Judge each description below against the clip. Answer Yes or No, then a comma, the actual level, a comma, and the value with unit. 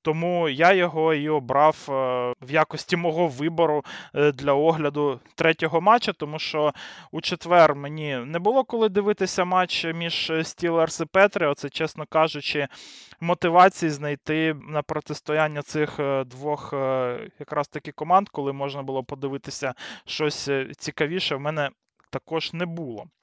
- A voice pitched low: No, medium, 155 Hz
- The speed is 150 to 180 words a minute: No, average, 125 wpm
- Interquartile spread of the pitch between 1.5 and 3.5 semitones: Yes, average, 2.7 semitones